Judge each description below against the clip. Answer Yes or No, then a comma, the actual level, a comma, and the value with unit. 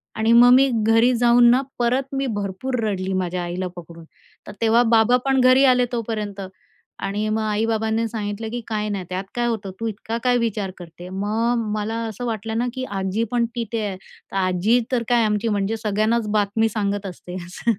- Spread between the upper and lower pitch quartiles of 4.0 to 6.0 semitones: No, average, 2.9 semitones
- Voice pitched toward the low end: No, high, 220 Hz